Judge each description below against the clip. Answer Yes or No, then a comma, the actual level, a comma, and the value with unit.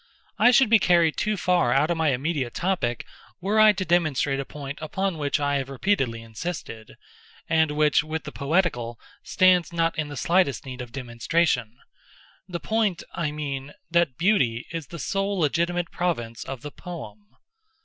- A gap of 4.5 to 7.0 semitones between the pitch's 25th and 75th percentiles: Yes, average, 4.9 semitones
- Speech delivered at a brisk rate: No, average, 165 wpm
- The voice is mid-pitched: Yes, medium, 155 Hz